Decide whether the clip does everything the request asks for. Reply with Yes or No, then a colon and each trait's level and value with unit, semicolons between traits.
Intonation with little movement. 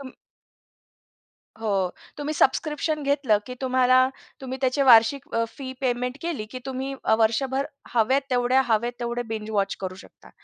No: average, 3.1 semitones